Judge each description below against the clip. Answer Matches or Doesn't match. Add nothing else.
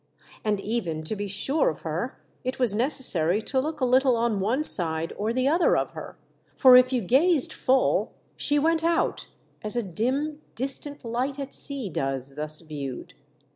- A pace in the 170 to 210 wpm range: Matches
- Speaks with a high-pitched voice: Matches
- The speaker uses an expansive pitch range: Matches